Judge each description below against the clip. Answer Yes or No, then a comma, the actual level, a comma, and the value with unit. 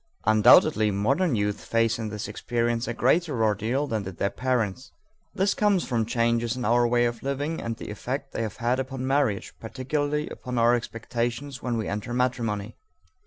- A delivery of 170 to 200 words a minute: Yes, average, 180 wpm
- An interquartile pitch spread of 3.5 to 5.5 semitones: No, average, 3.0 semitones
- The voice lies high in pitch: No, low, 120 Hz